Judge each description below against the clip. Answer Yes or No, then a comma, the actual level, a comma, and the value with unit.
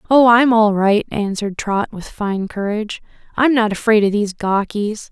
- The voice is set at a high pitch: Yes, high, 215 Hz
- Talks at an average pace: Yes, average, 175 wpm